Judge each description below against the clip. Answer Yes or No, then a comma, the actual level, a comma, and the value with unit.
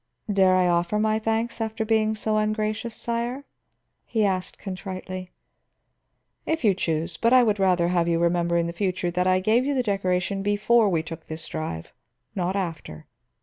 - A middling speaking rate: Yes, average, 175 wpm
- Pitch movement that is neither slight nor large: Yes, average, 3.9 semitones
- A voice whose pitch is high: Yes, high, 195 Hz